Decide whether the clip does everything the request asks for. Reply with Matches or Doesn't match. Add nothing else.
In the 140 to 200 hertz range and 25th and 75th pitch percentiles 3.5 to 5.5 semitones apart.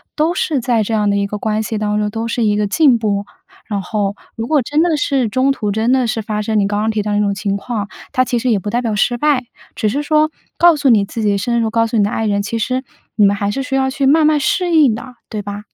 Doesn't match